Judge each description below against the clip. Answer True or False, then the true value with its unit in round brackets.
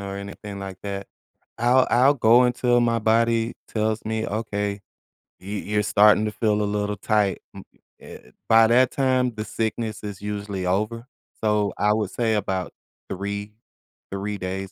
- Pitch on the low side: True (105 Hz)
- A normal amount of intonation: False (2.2 semitones)